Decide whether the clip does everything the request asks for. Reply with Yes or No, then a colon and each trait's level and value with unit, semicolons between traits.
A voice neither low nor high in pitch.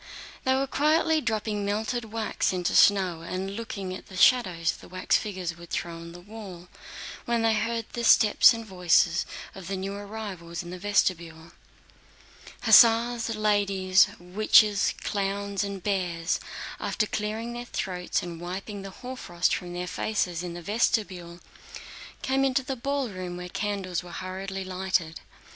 No: high, 195 Hz